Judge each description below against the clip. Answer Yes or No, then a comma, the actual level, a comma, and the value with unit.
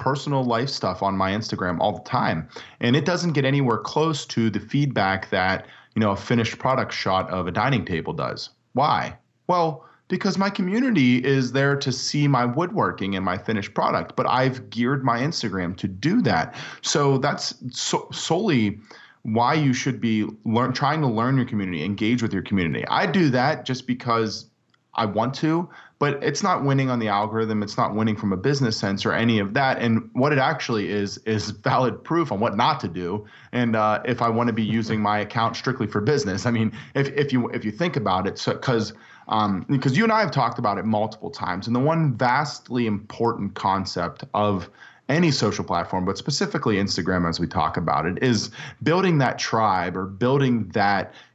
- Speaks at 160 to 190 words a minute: No, average, 200 wpm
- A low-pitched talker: Yes, low, 115 Hz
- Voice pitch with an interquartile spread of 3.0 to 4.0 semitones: No, average, 4.8 semitones